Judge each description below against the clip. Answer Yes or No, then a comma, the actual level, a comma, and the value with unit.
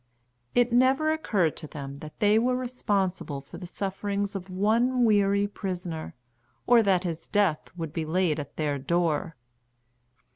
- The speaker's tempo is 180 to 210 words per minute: No, average, 150 wpm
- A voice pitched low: No, high, 190 Hz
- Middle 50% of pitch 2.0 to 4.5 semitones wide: No, average, 5.1 semitones